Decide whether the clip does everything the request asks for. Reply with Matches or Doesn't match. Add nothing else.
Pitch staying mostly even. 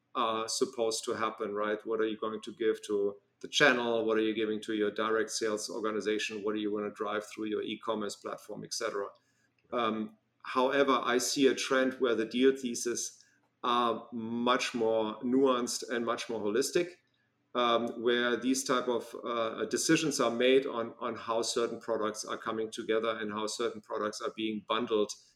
Matches